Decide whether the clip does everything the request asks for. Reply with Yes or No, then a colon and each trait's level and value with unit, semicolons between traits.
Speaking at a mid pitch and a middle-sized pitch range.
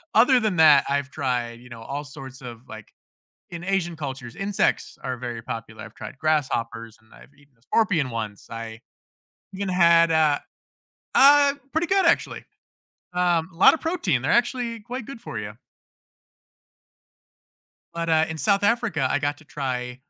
No: medium, 150 Hz; wide, 8.0 semitones